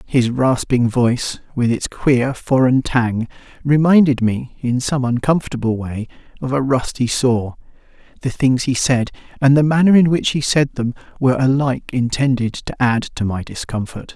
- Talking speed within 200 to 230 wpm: No, average, 155 wpm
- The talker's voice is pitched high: No, low, 130 Hz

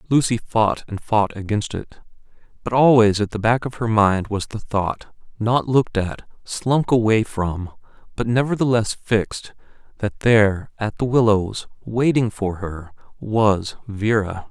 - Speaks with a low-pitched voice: Yes, low, 110 Hz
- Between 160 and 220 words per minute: No, average, 150 wpm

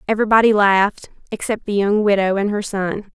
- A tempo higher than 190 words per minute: No, average, 170 wpm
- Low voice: No, high, 205 Hz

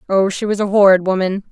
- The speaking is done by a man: No, female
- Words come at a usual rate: No, fast, 235 wpm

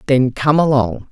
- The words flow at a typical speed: Yes, average, 160 wpm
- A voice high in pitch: No, low, 135 Hz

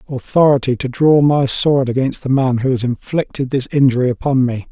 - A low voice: Yes, low, 130 Hz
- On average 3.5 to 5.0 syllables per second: No, 5.4 syllables/s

